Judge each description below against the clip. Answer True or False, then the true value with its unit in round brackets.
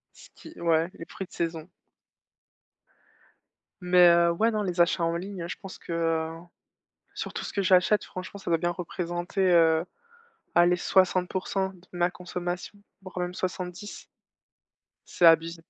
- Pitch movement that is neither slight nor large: False (1.6 semitones)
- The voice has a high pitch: False (175 Hz)